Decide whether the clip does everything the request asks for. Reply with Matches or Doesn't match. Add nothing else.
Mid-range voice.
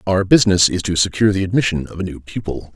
Doesn't match